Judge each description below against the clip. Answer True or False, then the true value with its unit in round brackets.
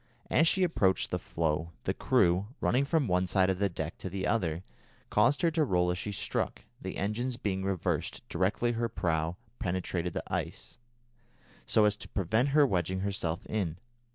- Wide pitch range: False (4.7 semitones)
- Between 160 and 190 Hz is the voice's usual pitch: False (95 Hz)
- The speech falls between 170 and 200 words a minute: True (180 wpm)